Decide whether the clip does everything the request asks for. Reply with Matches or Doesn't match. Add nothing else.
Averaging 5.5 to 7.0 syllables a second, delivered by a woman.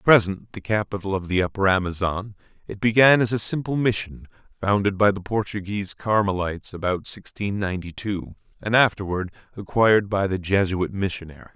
Doesn't match